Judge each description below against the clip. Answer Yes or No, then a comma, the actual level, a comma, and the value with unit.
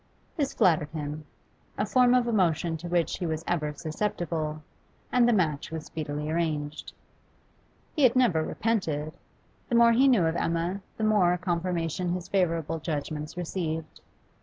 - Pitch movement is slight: No, average, 4.8 semitones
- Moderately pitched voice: Yes, medium, 170 Hz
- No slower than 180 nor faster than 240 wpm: No, average, 150 wpm